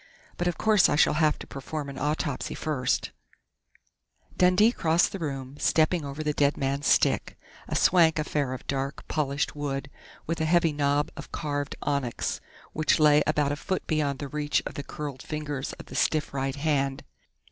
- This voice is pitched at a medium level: Yes, medium, 145 Hz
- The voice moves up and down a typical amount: No, narrow, 2.0 semitones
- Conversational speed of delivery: Yes, average, 180 wpm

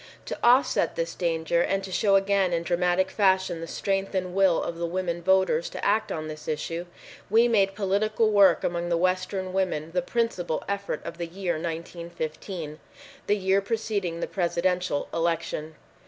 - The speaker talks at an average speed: Yes, average, 170 wpm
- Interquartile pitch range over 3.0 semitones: No, narrow, 2.6 semitones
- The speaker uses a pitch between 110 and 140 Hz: No, medium, 185 Hz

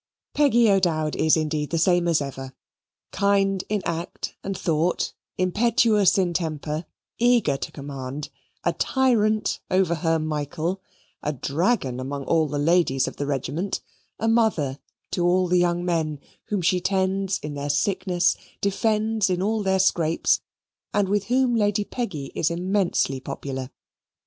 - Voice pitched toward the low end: No, medium, 175 Hz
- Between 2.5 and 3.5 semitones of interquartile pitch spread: No, average, 4.9 semitones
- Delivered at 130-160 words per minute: Yes, average, 145 wpm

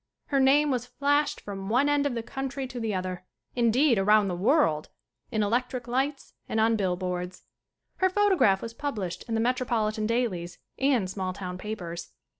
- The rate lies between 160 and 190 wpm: Yes, average, 180 wpm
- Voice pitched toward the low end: No, high, 230 Hz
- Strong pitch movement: Yes, wide, 5.8 semitones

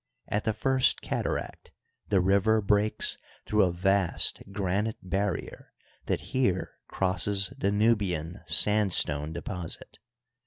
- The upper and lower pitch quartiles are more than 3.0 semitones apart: No, average, 2.7 semitones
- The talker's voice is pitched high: No, low, 100 Hz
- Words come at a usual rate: No, slow, 115 wpm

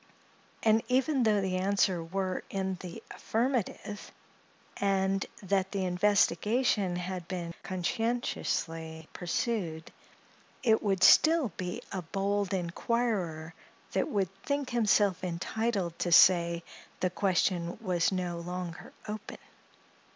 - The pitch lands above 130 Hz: Yes, high, 190 Hz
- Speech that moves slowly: Yes, slow, 110 wpm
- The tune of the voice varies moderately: Yes, average, 3.4 semitones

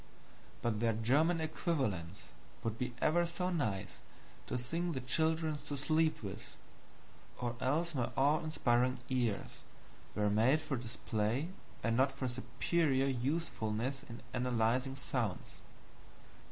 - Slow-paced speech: Yes, slow, 125 wpm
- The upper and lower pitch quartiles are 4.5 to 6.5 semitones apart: Yes, average, 5.0 semitones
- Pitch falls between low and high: No, low, 130 Hz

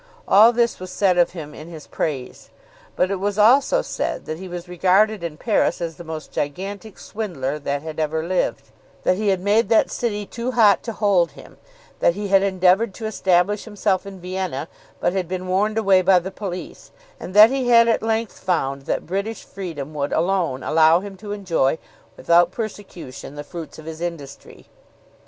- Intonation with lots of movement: No, average, 3.9 semitones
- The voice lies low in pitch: No, medium, 185 Hz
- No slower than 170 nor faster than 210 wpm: Yes, average, 190 wpm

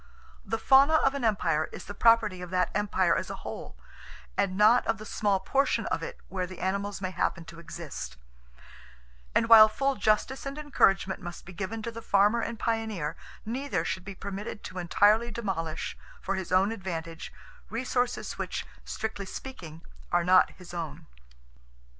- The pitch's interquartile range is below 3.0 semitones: No, average, 4.0 semitones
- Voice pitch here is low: No, high, 200 Hz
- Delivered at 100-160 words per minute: No, average, 170 wpm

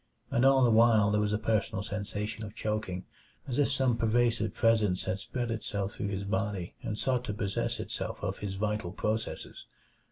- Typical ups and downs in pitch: No, narrow, 2.1 semitones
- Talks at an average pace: Yes, average, 185 wpm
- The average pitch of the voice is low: Yes, low, 105 Hz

